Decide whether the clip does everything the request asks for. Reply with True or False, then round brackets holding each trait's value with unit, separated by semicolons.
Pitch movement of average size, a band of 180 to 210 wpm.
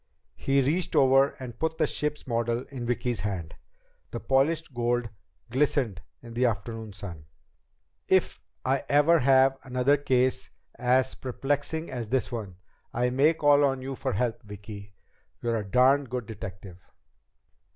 False (3.3 semitones; 145 wpm)